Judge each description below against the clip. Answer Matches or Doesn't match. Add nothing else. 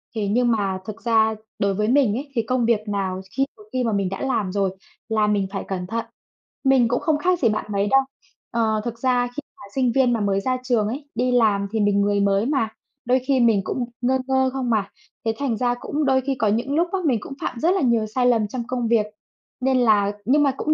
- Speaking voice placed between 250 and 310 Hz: Doesn't match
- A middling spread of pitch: Matches